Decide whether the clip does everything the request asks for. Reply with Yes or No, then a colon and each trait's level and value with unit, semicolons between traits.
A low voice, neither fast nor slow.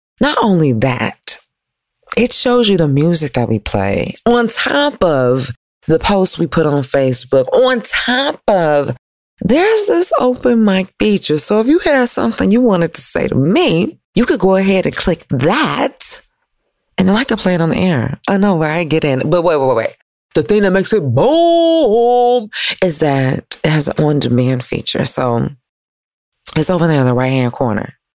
No: medium, 175 Hz; average, 190 wpm